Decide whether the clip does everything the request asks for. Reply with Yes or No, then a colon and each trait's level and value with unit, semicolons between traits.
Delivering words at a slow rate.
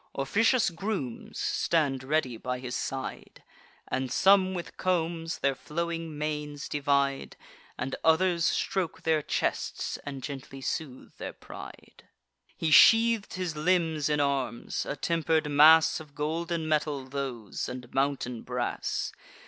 Yes: slow, 125 wpm